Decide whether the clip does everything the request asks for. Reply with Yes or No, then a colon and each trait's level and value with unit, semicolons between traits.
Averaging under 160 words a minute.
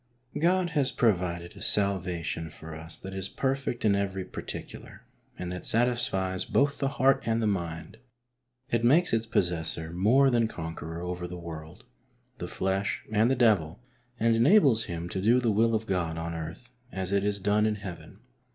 No: average, 180 wpm